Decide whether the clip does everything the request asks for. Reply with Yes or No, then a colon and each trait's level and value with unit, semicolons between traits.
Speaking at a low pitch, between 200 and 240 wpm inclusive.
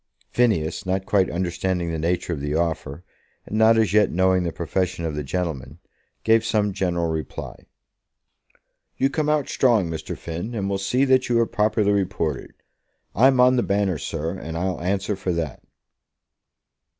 No: very low, 95 Hz; average, 165 wpm